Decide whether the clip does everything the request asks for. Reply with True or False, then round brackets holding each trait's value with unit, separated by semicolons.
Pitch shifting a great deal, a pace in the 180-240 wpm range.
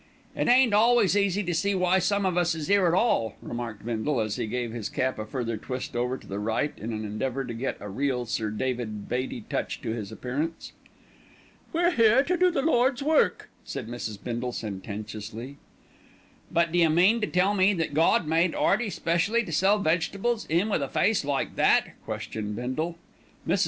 True (9.0 semitones; 195 wpm)